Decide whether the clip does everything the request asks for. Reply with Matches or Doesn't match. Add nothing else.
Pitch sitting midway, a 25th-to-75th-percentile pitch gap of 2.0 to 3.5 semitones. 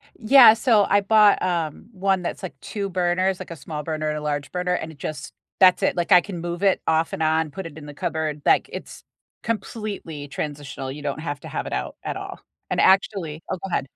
Doesn't match